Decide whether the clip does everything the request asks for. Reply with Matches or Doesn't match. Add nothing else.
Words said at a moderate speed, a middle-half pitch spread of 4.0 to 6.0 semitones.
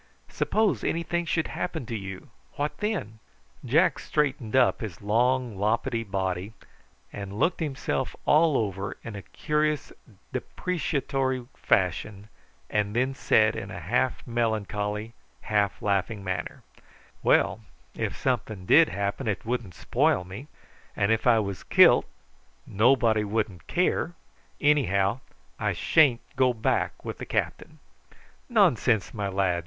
Doesn't match